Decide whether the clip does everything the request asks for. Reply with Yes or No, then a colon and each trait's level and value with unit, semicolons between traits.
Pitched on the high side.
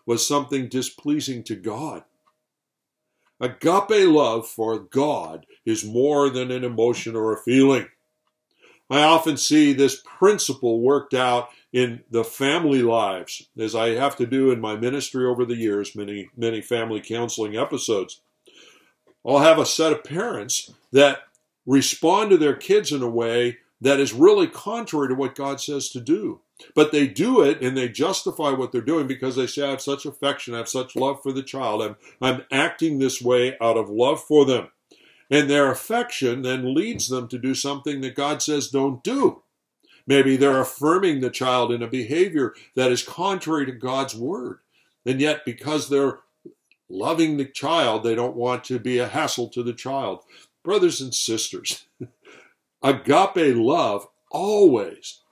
No: low, 130 Hz